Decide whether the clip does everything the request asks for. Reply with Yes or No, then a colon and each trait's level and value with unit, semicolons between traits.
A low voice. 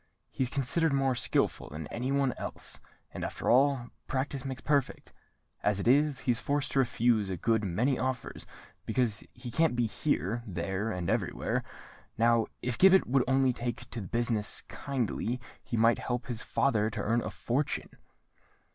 Yes: low, 120 Hz